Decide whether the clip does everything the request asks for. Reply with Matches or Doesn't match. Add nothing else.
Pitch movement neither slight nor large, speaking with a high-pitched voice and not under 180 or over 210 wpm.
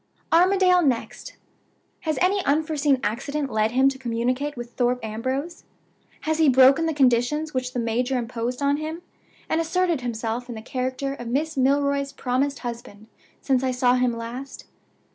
Doesn't match